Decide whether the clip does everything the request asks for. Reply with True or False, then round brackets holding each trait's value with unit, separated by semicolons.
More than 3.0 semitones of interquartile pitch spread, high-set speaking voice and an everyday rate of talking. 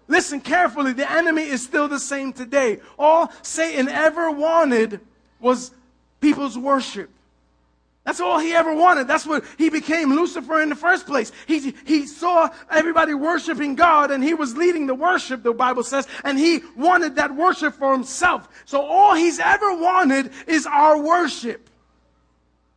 True (3.9 semitones; 295 Hz; 160 wpm)